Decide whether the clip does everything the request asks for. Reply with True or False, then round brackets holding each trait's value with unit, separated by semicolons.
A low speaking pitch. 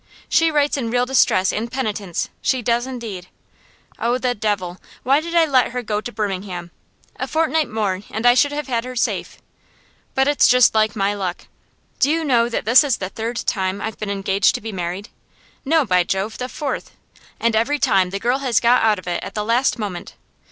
False (230 Hz)